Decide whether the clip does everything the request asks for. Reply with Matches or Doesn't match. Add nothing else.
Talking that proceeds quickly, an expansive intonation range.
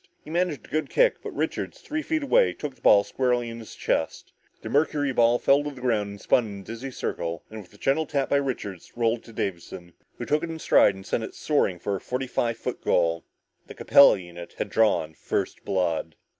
Matches